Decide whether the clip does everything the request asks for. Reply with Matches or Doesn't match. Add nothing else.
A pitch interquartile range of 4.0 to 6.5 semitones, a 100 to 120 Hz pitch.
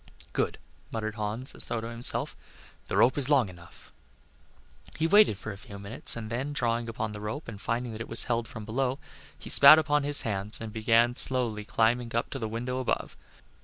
Doesn't match